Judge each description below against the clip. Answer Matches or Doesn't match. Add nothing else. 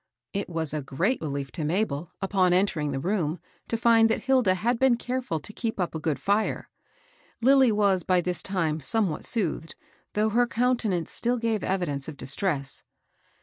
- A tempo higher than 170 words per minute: Matches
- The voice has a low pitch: Doesn't match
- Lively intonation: Matches